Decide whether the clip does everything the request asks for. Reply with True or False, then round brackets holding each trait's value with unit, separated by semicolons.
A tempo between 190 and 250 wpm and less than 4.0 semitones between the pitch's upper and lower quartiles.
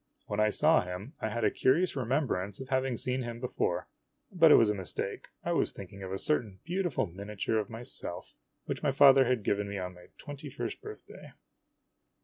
False (195 wpm; 5.3 semitones)